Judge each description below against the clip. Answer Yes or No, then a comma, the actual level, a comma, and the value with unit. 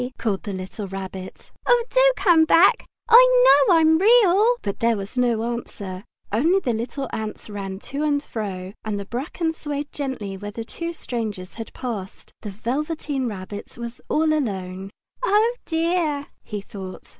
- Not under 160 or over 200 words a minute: Yes, average, 165 wpm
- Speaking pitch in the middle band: No, high, 240 Hz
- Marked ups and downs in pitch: Yes, wide, 8.0 semitones